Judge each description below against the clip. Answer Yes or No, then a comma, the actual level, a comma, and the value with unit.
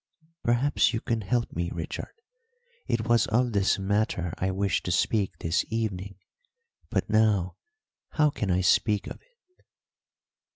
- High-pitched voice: No, low, 105 Hz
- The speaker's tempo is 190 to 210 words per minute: No, average, 140 wpm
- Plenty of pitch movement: No, average, 3.9 semitones